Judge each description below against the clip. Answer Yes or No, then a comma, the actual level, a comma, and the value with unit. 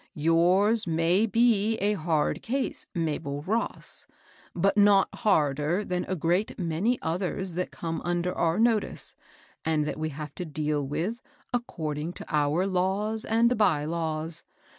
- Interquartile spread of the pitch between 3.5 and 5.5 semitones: Yes, average, 4.7 semitones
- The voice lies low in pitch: No, medium, 175 Hz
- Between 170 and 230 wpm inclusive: No, average, 145 wpm